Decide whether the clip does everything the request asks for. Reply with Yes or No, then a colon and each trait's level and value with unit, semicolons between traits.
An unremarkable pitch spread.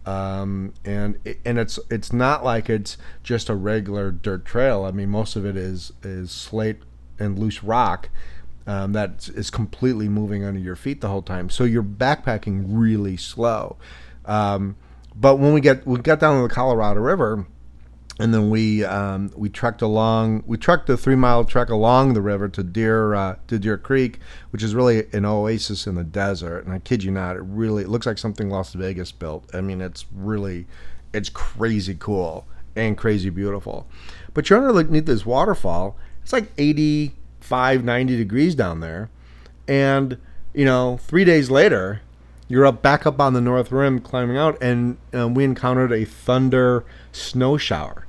Yes: average, 4.7 semitones